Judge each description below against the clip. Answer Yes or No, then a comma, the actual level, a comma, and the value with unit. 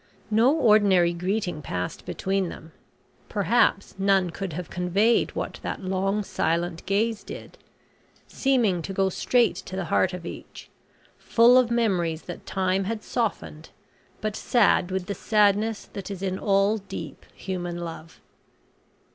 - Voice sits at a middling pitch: No, high, 195 Hz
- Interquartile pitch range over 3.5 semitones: No, average, 3.2 semitones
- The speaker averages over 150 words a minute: No, average, 140 wpm